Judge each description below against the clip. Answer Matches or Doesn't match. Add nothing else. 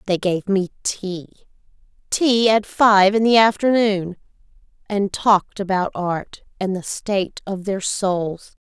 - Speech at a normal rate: Doesn't match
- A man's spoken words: Doesn't match